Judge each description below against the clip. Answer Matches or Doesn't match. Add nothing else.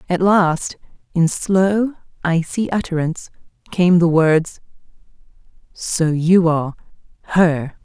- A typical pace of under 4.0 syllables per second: Matches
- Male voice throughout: Doesn't match